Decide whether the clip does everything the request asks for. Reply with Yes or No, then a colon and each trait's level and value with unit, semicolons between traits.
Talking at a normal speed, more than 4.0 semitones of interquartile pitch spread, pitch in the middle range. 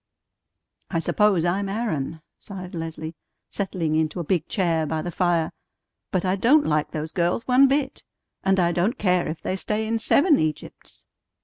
Yes: average, 170 wpm; average, 4.4 semitones; medium, 180 Hz